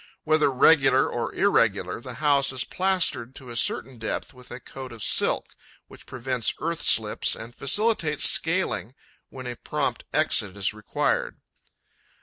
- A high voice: No, low, 130 Hz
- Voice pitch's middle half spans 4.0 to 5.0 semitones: Yes, average, 4.6 semitones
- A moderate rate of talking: Yes, average, 145 wpm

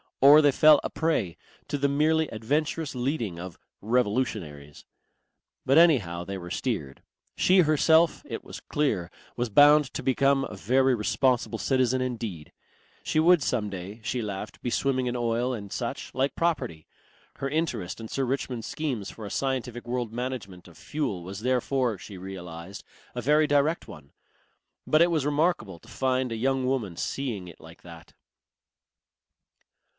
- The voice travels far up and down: Yes, wide, 5.9 semitones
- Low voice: Yes, low, 125 Hz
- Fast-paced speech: No, average, 160 wpm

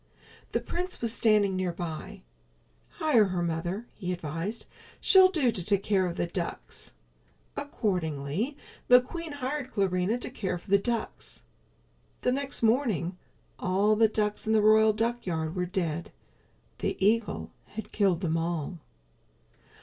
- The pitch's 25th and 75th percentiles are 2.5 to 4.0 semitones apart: No, average, 4.8 semitones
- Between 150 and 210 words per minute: No, average, 140 wpm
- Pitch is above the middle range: Yes, high, 200 Hz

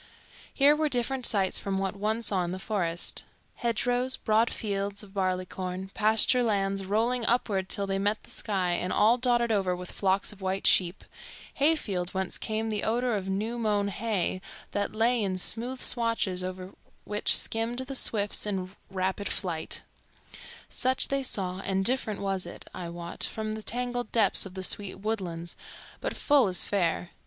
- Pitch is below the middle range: No, high, 205 Hz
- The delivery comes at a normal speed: Yes, average, 170 wpm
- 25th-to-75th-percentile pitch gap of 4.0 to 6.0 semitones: No, average, 3.5 semitones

